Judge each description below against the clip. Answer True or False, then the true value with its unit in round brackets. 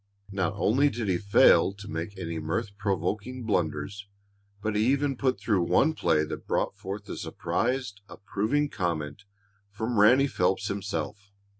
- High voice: False (100 Hz)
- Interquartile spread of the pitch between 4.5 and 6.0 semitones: False (4.1 semitones)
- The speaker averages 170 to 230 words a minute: False (150 wpm)